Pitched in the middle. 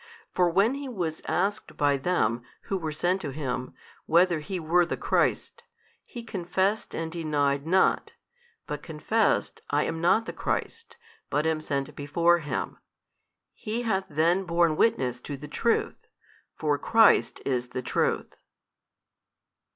Yes: medium, 165 Hz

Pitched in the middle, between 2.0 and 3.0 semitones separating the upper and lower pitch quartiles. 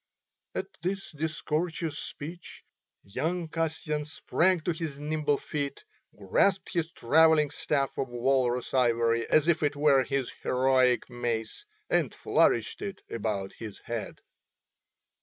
No: medium, 145 Hz; average, 4.4 semitones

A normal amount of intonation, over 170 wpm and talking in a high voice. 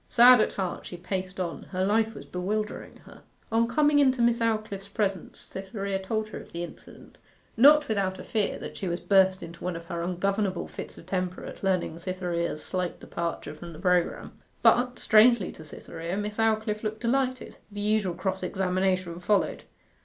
Yes: average, 3.2 semitones; average, 180 wpm; high, 195 Hz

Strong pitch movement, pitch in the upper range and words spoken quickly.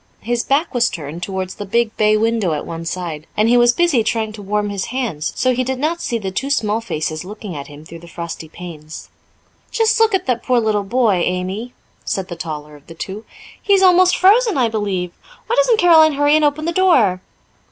Yes: wide, 7.4 semitones; high, 220 Hz; fast, 220 wpm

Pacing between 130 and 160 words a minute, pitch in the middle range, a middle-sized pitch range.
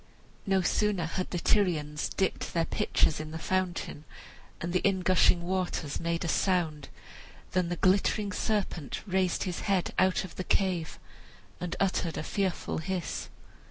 No: average, 155 wpm; medium, 180 Hz; narrow, 2.2 semitones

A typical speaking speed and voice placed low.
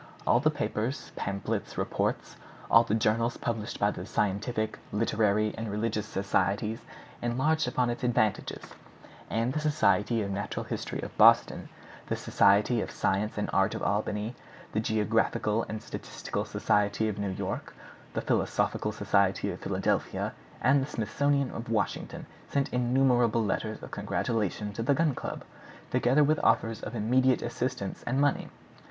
Yes: average, 145 wpm; low, 115 Hz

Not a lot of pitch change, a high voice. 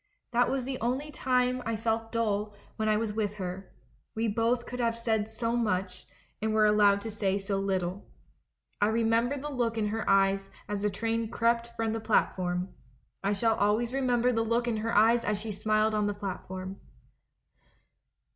Yes: narrow, 2.3 semitones; high, 220 Hz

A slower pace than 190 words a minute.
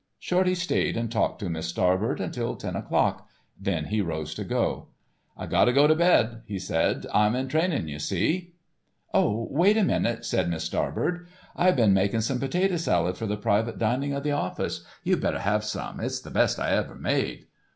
No: average, 195 wpm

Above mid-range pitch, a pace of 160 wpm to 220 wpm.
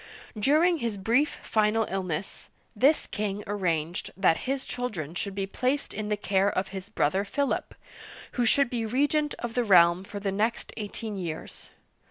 Yes: high, 210 Hz; average, 165 wpm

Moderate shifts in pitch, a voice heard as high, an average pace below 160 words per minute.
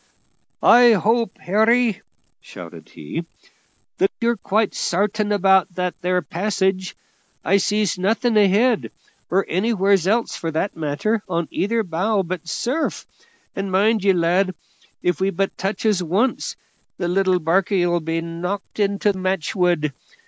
Yes: average, 3.2 semitones; high, 195 Hz; slow, 135 wpm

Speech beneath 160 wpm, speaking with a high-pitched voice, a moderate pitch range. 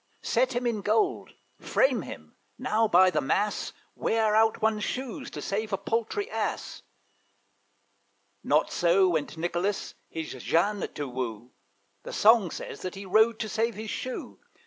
Yes: average, 150 wpm; high, 210 Hz; average, 4.0 semitones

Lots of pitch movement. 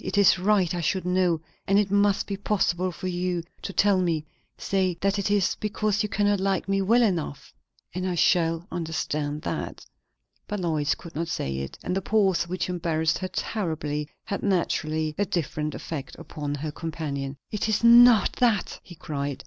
No: average, 4.0 semitones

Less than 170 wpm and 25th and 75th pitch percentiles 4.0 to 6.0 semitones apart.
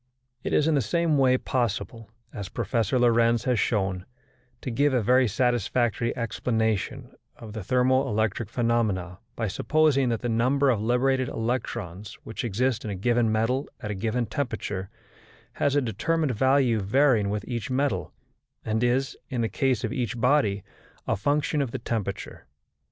No: average, 160 wpm; average, 3.2 semitones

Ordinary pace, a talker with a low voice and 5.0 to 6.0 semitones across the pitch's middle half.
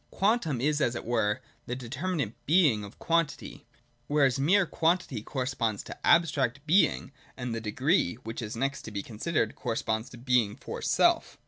Yes: average, 160 wpm; low, 130 Hz; wide, 5.4 semitones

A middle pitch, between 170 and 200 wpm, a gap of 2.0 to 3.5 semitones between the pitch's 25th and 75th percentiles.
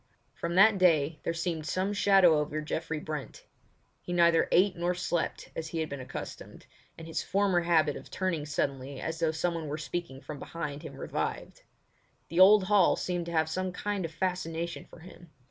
Yes: medium, 170 Hz; average, 185 wpm; average, 2.7 semitones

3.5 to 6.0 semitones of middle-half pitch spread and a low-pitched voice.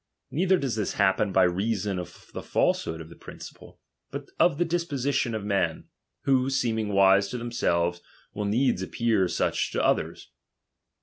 Yes: average, 5.2 semitones; low, 105 Hz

